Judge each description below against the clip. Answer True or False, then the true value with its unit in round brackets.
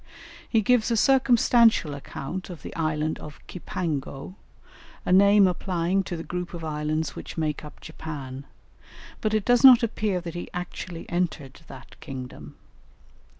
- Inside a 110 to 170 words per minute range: True (150 wpm)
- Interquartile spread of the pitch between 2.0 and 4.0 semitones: False (4.8 semitones)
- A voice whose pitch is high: False (175 Hz)